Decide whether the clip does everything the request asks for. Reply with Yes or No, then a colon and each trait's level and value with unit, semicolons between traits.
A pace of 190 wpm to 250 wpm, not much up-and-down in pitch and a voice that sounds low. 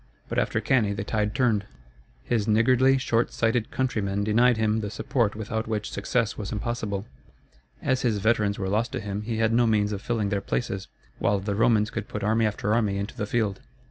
Yes: average, 200 wpm; narrow, 2.2 semitones; low, 110 Hz